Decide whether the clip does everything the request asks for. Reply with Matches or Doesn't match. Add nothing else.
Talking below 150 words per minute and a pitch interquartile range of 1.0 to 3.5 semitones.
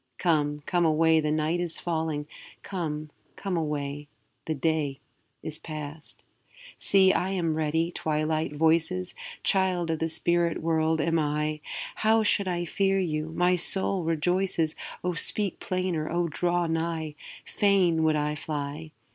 Matches